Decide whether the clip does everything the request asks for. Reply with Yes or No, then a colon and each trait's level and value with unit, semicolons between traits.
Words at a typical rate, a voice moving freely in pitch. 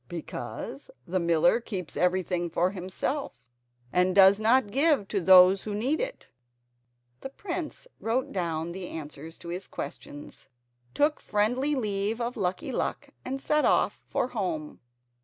Yes: average, 145 wpm; wide, 6.1 semitones